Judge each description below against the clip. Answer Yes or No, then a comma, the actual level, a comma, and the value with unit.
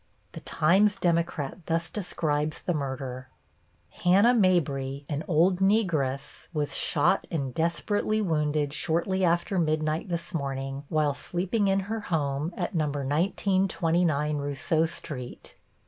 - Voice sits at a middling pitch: Yes, medium, 160 Hz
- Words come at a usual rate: No, slow, 120 wpm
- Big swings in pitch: No, average, 4.0 semitones